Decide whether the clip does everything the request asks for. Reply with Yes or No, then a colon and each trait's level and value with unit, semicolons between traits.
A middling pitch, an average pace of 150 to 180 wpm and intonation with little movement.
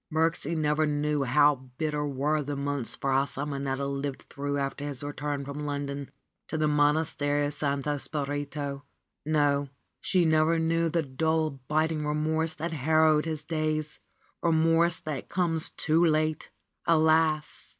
No: medium, 150 Hz; average, 140 wpm; narrow, 1.9 semitones